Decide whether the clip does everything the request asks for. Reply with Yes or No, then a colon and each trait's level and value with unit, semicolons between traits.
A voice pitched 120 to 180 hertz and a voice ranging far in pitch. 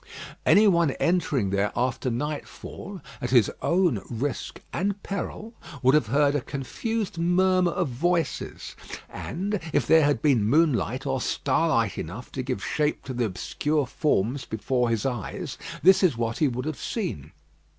Yes: medium, 140 Hz; wide, 6.2 semitones